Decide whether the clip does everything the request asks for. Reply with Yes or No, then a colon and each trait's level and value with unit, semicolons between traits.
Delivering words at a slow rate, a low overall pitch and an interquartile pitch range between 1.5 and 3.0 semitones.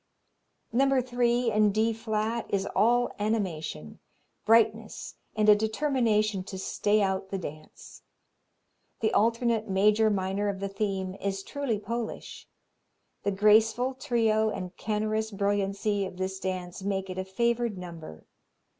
No: slow, 130 wpm; high, 210 Hz; average, 2.7 semitones